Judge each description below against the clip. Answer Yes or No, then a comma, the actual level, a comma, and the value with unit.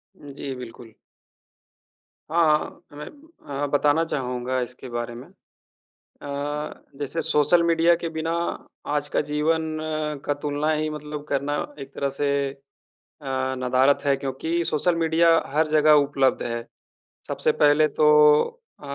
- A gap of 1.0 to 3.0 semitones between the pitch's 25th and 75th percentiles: Yes, narrow, 2.4 semitones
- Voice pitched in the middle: Yes, medium, 145 Hz